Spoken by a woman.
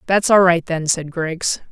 Yes: female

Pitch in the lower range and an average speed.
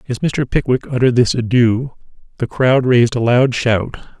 Yes: low, 125 Hz; average, 170 wpm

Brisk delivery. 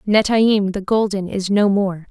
No: average, 170 wpm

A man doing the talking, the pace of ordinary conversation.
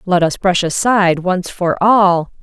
No: female; average, 175 wpm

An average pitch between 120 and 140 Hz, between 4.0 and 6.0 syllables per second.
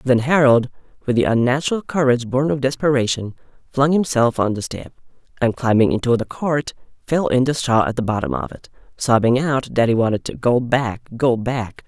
Yes: low, 125 Hz; 5.3 syllables/s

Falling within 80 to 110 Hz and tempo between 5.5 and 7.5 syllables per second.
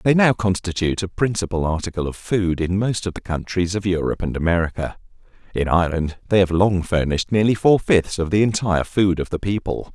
Yes: very low, 95 Hz; 5.9 syllables/s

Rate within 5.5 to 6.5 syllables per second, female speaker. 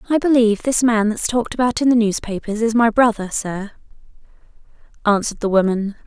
Yes: 6.0 syllables/s; female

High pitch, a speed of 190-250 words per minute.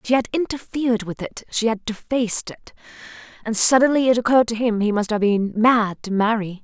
Yes: high, 225 Hz; average, 200 wpm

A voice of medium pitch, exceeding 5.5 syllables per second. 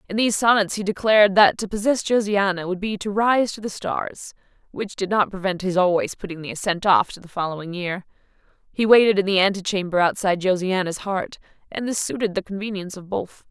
No: high, 195 Hz; 5.8 syllables/s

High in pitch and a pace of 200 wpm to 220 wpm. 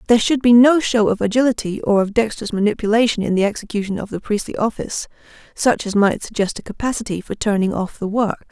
Yes: high, 215 Hz; fast, 205 wpm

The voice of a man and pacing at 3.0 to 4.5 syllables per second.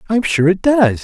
Yes: male; 4.4 syllables/s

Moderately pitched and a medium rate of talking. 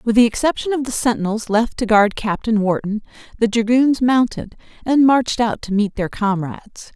No: high, 225 Hz; average, 180 wpm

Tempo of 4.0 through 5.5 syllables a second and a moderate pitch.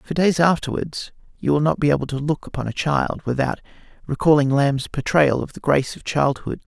Yes: 5.4 syllables/s; medium, 145 Hz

